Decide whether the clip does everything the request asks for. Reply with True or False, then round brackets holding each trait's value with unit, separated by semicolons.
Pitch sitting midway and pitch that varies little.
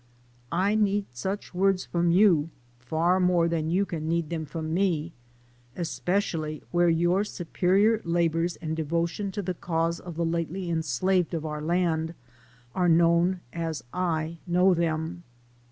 True (170 Hz; 2.1 semitones)